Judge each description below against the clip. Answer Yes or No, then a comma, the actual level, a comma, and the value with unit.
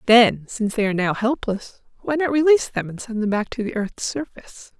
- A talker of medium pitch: No, high, 230 Hz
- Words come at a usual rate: No, fast, 225 wpm